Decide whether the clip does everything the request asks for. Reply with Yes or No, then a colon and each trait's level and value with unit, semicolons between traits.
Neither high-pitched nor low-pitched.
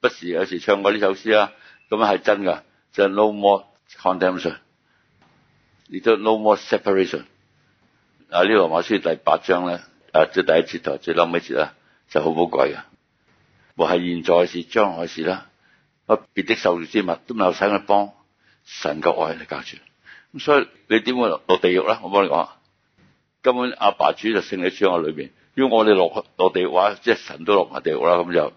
No: low, 100 Hz